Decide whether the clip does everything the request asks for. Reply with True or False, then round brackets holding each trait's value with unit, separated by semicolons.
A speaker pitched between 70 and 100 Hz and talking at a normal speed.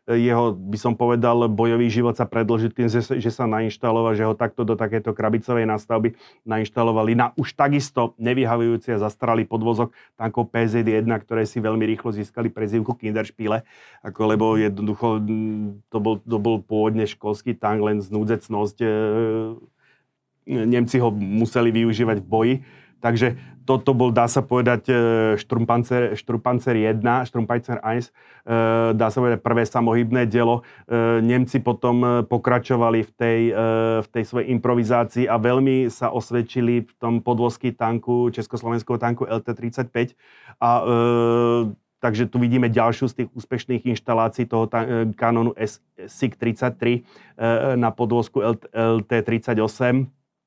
False (115 Hz; 125 wpm)